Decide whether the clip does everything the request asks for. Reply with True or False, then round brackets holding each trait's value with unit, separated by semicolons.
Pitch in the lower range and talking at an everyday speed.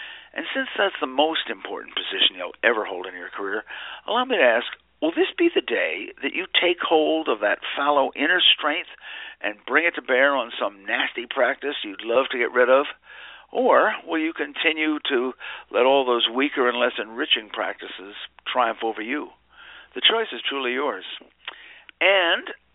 False (175 Hz; 180 wpm)